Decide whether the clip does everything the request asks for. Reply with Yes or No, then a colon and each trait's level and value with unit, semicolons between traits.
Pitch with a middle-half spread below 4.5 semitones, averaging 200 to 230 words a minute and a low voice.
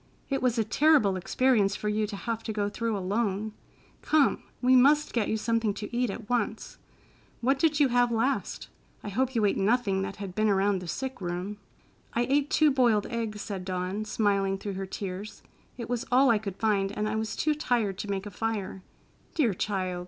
No: average, 3.7 semitones; fast, 205 wpm; high, 215 Hz